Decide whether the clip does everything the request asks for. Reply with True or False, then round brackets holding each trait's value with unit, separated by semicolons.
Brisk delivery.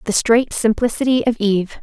False (165 wpm)